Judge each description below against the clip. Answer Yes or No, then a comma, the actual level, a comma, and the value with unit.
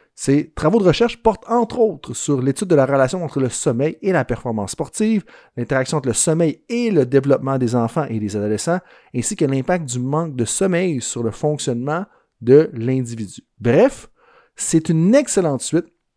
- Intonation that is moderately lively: No, wide, 5.9 semitones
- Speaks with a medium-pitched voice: Yes, medium, 150 Hz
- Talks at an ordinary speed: Yes, average, 180 wpm